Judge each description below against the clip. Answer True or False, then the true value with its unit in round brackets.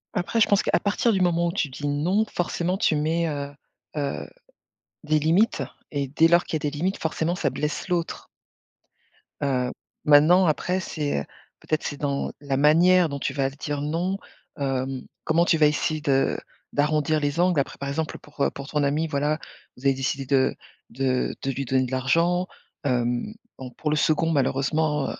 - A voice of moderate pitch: True (150 Hz)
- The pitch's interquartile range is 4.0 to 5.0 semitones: False (3.2 semitones)